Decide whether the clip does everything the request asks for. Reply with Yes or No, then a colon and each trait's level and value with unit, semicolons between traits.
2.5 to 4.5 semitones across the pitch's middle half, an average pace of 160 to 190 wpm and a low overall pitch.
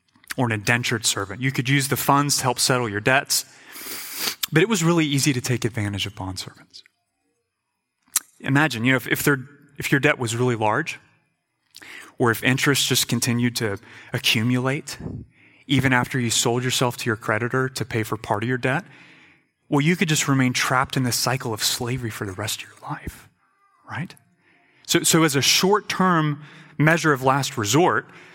Yes: average, 3.5 semitones; average, 180 wpm; low, 130 Hz